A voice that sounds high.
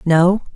No: medium, 180 Hz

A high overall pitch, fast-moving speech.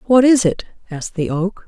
Yes: high, 205 Hz; fast, 215 wpm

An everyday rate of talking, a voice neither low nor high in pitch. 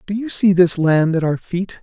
No: fast, 265 wpm; medium, 180 Hz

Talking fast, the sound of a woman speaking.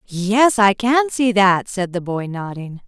No: average, 190 wpm; female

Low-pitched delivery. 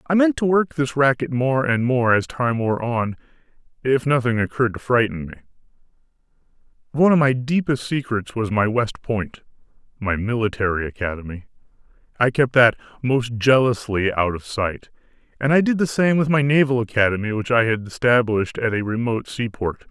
Yes: low, 120 Hz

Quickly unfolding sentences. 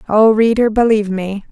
No: average, 160 wpm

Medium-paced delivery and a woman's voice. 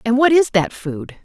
No: fast, 240 wpm; female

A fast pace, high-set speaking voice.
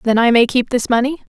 Yes: fast, 265 wpm; high, 245 Hz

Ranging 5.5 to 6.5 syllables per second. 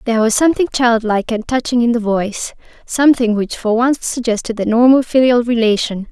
Yes: 6.0 syllables/s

